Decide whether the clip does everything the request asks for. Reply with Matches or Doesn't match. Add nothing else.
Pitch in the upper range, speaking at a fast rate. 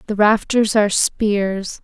Doesn't match